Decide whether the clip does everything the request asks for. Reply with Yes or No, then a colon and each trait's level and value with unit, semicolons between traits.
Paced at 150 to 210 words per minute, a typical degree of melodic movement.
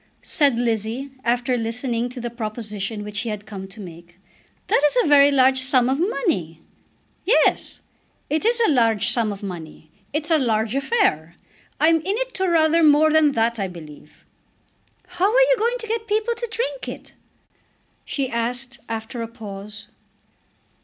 No: average, 160 wpm; wide, 6.7 semitones